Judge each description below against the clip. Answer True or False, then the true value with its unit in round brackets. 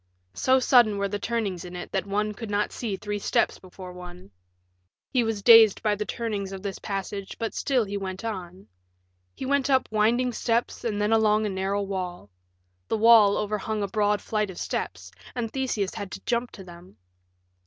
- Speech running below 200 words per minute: True (190 wpm)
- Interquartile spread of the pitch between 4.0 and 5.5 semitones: False (2.8 semitones)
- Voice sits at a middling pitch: False (210 Hz)